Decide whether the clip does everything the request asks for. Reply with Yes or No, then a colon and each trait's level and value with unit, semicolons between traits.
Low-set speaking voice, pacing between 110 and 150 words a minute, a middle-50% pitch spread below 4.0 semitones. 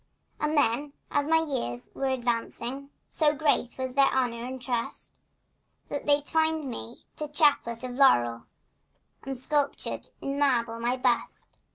No: very high, 265 Hz; average, 145 wpm; average, 3.5 semitones